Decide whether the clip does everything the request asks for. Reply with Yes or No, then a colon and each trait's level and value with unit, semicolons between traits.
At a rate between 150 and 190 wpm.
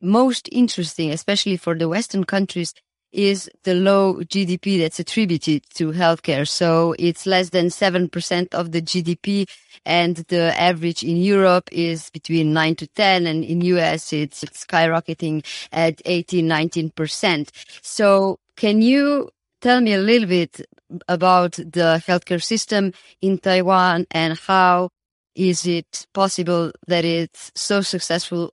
No: slow, 135 wpm